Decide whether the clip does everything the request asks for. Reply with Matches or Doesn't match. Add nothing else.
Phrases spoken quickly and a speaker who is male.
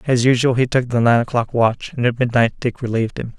Matches